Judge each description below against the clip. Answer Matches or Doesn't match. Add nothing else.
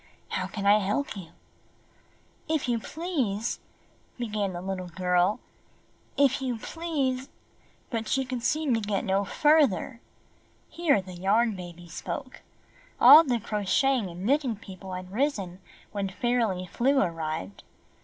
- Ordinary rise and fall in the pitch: Doesn't match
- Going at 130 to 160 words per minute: Matches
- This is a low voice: Doesn't match